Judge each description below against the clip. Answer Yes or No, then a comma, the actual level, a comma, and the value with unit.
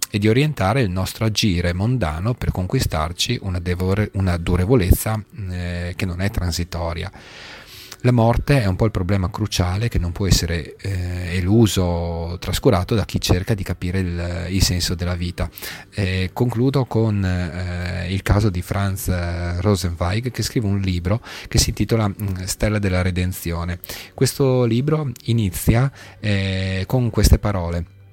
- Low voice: Yes, very low, 95 Hz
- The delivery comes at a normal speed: Yes, average, 150 wpm